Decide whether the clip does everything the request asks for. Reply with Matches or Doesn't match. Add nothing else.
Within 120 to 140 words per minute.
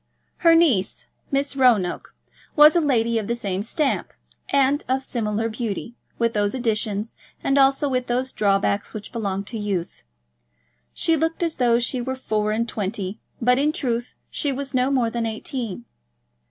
Doesn't match